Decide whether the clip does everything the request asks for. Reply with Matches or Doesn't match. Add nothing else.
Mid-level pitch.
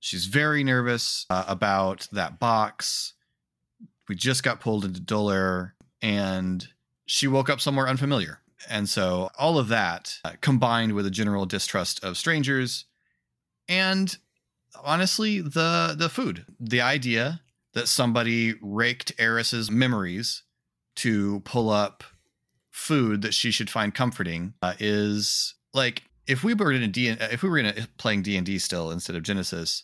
Doesn't match